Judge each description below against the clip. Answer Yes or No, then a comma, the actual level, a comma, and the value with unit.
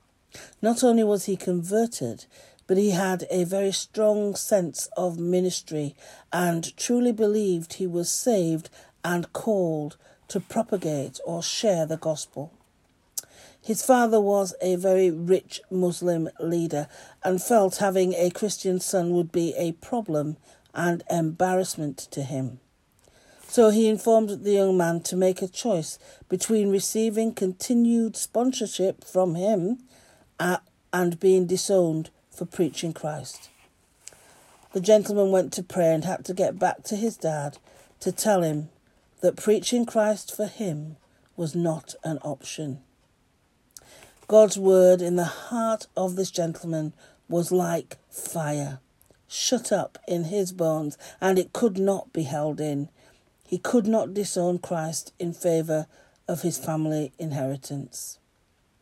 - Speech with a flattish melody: No, average, 4.0 semitones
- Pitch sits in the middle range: Yes, medium, 180 Hz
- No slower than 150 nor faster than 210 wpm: No, slow, 135 wpm